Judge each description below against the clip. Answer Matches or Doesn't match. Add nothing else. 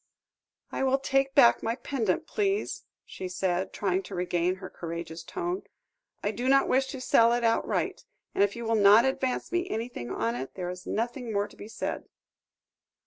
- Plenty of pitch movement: Matches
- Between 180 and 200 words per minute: Matches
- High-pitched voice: Matches